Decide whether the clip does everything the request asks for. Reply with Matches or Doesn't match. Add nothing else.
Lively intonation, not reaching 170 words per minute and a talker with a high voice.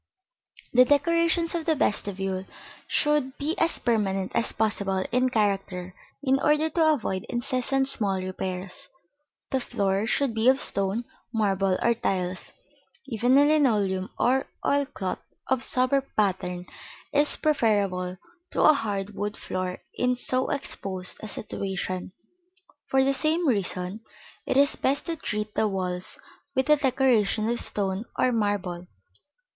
Matches